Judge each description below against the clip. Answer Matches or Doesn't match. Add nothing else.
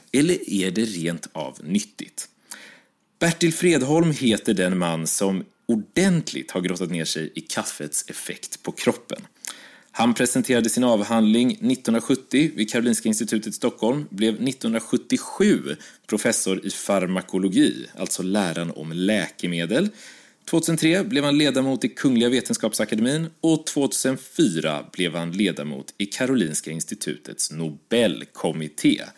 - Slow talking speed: Matches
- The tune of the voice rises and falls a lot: Matches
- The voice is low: Matches